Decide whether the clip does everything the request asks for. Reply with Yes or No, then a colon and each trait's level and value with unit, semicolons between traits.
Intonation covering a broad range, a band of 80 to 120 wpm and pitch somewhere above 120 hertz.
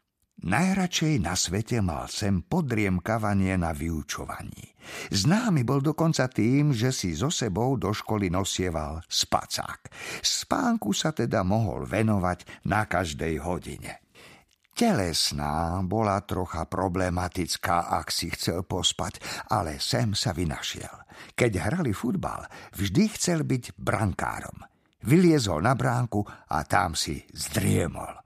No: wide, 6.2 semitones; average, 115 wpm; low, 100 Hz